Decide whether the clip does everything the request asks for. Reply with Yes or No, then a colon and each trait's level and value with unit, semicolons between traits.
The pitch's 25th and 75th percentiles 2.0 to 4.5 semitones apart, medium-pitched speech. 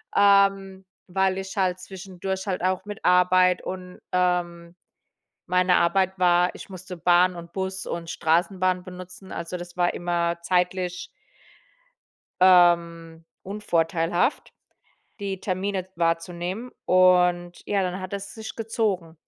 No: narrow, 1.5 semitones; medium, 180 Hz